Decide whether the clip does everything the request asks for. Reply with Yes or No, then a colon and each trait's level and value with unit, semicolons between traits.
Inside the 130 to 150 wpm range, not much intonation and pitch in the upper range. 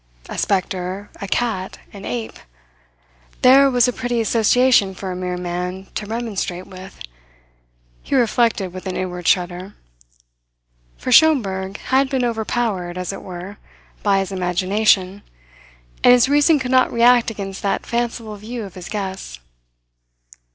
No: average, 140 wpm; average, 4.5 semitones; high, 200 Hz